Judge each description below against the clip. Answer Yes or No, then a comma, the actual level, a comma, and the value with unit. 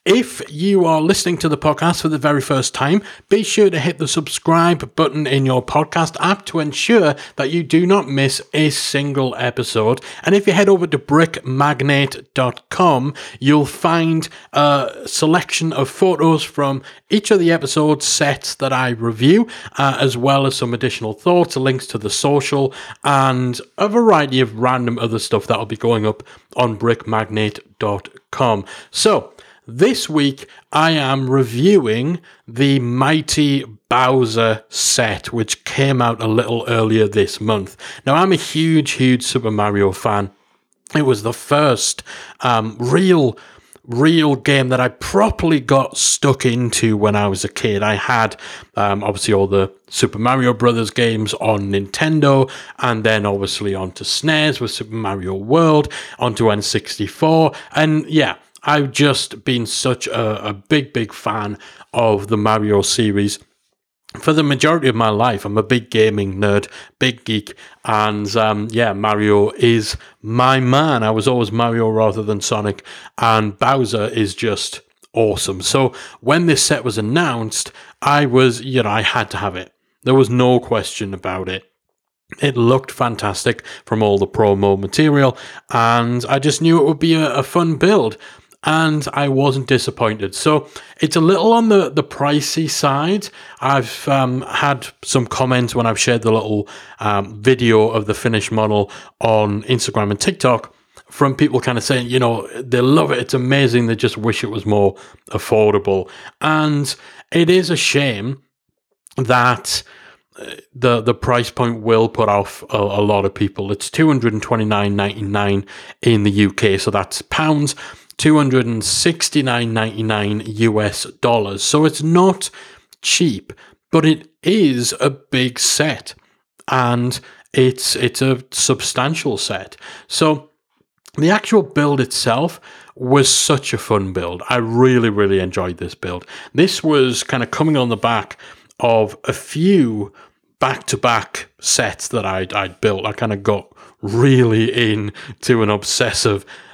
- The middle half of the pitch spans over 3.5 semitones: Yes, average, 5.2 semitones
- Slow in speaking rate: No, average, 155 wpm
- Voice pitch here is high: No, low, 125 Hz